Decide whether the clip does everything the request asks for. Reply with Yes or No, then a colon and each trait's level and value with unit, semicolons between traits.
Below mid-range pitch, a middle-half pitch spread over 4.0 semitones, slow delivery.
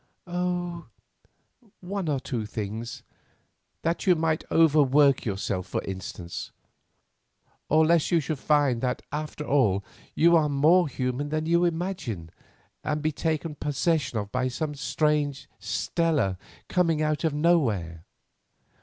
No: medium, 150 Hz; average, 4.7 semitones; slow, 130 wpm